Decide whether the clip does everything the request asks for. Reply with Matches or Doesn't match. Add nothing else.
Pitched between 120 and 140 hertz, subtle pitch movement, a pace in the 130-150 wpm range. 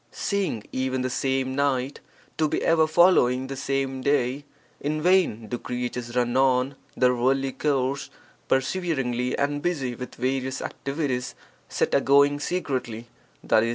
Matches